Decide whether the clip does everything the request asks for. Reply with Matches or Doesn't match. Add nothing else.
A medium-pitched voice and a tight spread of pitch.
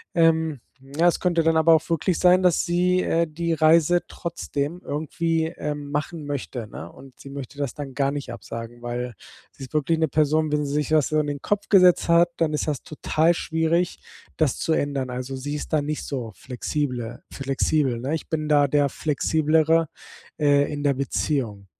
Doesn't match